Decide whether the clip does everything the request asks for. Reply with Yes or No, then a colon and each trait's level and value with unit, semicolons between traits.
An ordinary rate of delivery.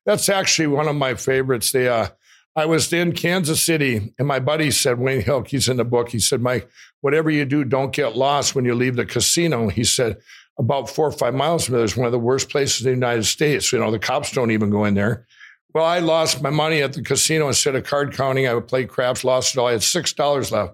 No: fast, 260 wpm